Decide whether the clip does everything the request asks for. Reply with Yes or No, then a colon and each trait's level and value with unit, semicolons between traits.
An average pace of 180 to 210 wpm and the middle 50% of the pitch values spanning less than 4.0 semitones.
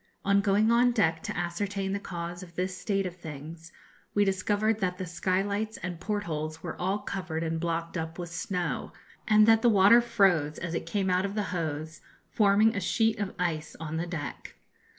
Yes: average, 195 wpm; average, 3.5 semitones